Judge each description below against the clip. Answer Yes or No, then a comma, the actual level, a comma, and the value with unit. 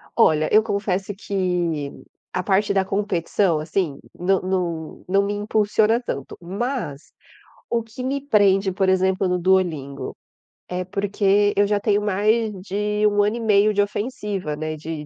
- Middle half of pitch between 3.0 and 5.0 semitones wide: No, narrow, 2.6 semitones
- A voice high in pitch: Yes, high, 195 Hz